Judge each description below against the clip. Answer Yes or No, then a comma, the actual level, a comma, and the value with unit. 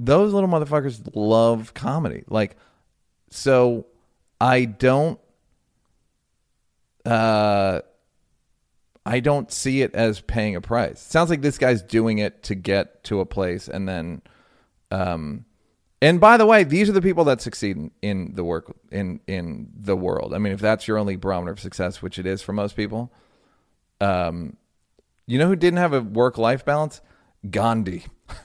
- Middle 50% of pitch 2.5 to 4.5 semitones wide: No, average, 5.3 semitones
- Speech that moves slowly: No, average, 160 wpm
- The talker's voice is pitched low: Yes, low, 110 Hz